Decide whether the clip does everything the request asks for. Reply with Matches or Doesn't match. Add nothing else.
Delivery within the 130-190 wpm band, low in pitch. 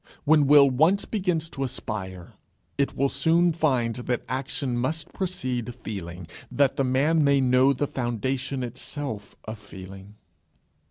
Matches